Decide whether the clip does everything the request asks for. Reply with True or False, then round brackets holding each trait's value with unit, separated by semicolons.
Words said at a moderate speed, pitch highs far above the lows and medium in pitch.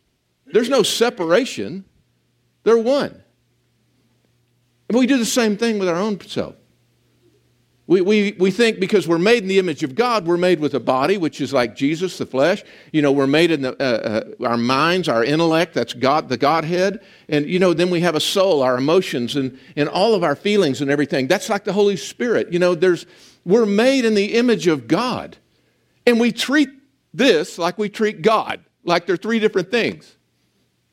True (190 wpm; 6.8 semitones; 180 Hz)